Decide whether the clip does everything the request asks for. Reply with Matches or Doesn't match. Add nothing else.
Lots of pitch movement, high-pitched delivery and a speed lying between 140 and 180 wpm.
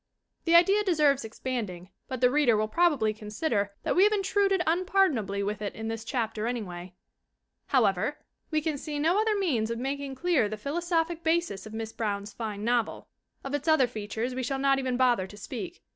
Doesn't match